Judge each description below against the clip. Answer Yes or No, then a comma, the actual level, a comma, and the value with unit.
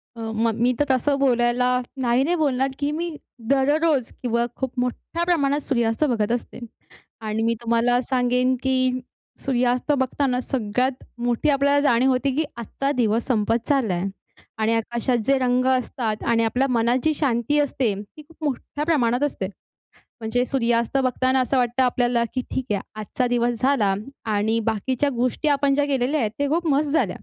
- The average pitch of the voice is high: Yes, very high, 250 Hz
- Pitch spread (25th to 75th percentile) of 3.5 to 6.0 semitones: No, average, 2.9 semitones